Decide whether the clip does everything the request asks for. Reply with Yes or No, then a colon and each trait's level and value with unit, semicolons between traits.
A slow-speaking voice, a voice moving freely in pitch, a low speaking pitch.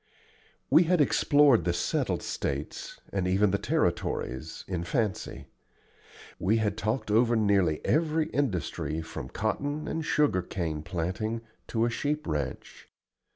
Yes: slow, 125 wpm; wide, 7.6 semitones; low, 105 Hz